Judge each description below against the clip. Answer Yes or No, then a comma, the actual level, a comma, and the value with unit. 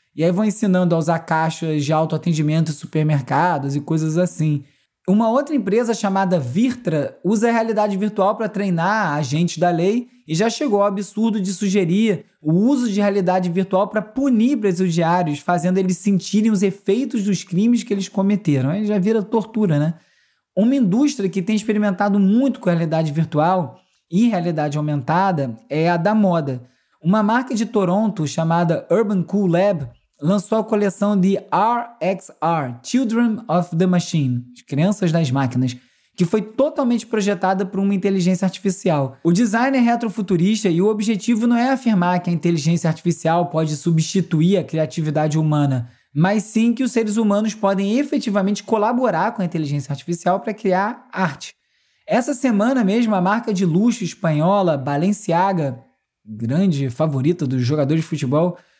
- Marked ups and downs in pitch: No, average, 4.9 semitones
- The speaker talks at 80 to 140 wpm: No, average, 155 wpm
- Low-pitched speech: No, high, 190 Hz